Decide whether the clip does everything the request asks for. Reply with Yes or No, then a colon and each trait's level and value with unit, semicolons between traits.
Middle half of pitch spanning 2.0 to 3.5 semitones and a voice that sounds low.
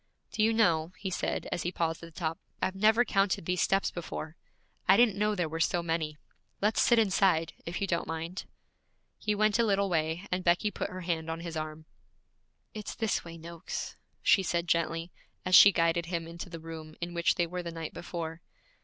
No: average, 3.0 semitones; medium, 170 Hz